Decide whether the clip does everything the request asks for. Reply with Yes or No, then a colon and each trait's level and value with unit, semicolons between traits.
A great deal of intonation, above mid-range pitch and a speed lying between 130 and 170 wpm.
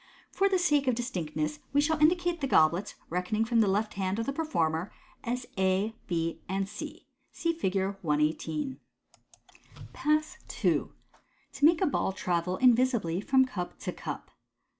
Yes: wide, 8.0 semitones; high, 215 Hz; average, 155 wpm